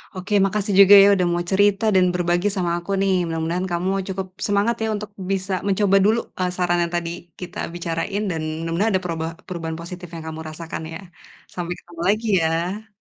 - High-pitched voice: No, medium, 180 Hz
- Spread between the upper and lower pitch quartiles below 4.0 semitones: Yes, average, 2.7 semitones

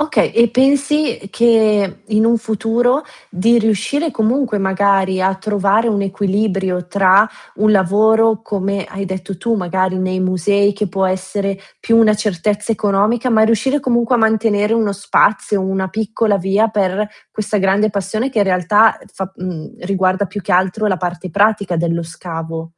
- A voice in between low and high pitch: No, high, 205 Hz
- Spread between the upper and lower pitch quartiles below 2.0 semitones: No, average, 2.7 semitones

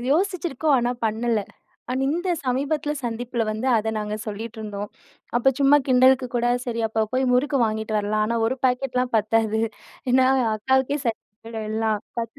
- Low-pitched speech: No, high, 240 Hz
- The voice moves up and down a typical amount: Yes, average, 3.2 semitones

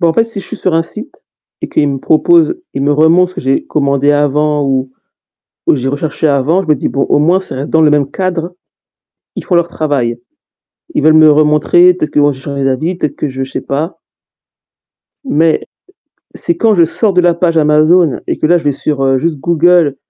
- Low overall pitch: No, medium, 155 Hz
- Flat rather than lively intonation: No, average, 3.7 semitones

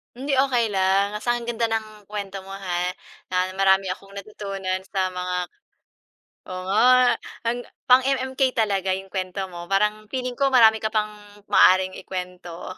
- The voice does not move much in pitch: No, average, 3.9 semitones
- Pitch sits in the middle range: No, high, 200 Hz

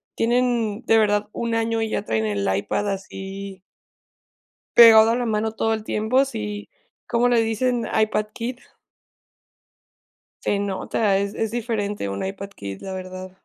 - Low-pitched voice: No, high, 215 Hz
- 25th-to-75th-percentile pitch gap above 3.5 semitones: No, average, 2.9 semitones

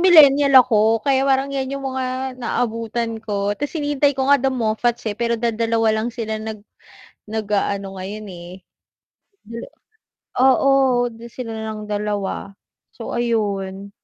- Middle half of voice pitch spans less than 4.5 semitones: Yes, average, 3.7 semitones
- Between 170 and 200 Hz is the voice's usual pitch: No, high, 230 Hz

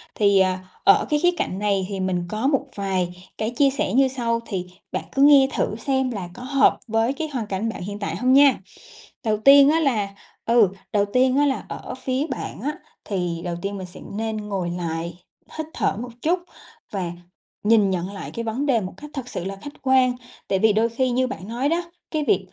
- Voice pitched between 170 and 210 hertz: No, high, 225 Hz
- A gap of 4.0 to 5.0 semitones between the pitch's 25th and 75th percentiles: No, wide, 5.5 semitones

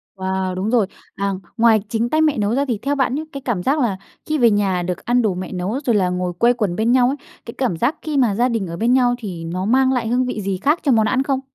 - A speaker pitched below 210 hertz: No, high, 230 Hz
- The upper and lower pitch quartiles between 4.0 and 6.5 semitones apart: Yes, average, 5.1 semitones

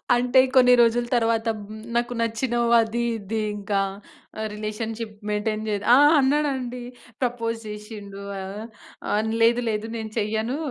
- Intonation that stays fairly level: Yes, narrow, 2.3 semitones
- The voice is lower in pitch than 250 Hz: Yes, high, 225 Hz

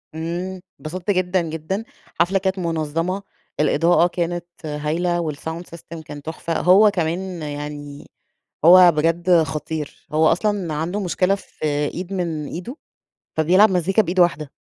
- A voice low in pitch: No, medium, 170 Hz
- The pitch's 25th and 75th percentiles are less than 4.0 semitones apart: Yes, average, 2.7 semitones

